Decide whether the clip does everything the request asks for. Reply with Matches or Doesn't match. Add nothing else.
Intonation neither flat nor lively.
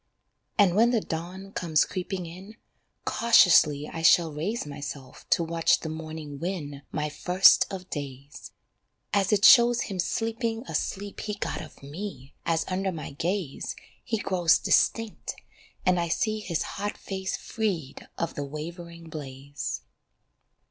Matches